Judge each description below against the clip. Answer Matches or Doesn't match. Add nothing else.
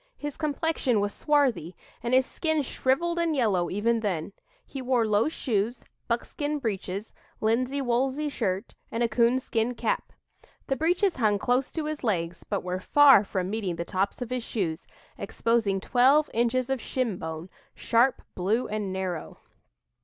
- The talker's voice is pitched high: Matches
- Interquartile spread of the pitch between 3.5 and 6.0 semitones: Matches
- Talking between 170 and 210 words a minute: Doesn't match